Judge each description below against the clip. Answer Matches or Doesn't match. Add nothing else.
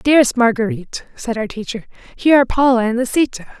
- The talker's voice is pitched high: Matches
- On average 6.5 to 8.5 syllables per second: Matches